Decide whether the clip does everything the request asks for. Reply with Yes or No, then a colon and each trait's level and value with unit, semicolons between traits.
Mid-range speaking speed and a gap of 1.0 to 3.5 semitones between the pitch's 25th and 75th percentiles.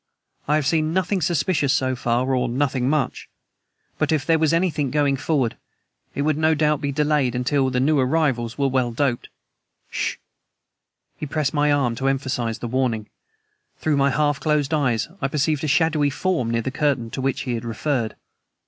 Yes: average, 185 wpm; average, 3.0 semitones